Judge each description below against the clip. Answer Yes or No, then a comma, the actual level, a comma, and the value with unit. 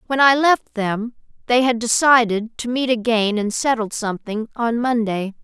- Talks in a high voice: Yes, high, 230 Hz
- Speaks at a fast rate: No, average, 165 wpm